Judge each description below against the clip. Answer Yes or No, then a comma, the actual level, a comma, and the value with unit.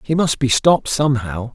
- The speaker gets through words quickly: No, average, 195 wpm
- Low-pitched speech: Yes, low, 130 Hz